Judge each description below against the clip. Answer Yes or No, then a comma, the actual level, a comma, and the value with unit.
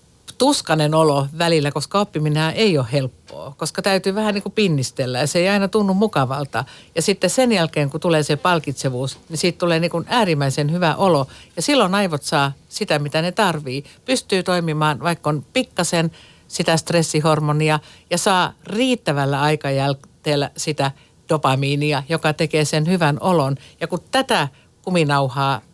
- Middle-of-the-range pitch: Yes, medium, 160 Hz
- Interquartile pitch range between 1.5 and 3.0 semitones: No, average, 4.1 semitones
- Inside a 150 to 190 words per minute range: Yes, fast, 155 wpm